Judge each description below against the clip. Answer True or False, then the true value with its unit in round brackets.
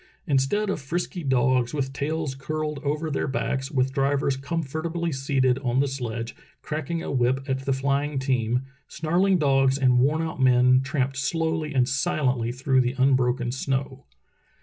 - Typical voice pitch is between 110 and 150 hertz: True (135 Hz)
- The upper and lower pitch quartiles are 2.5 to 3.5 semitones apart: True (2.8 semitones)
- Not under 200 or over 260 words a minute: False (155 wpm)